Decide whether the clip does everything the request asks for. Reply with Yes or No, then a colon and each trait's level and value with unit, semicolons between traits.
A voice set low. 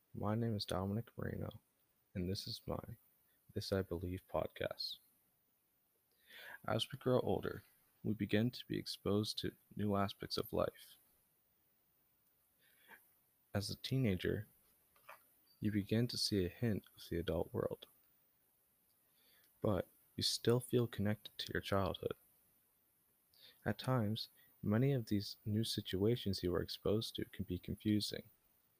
Yes: low, 105 Hz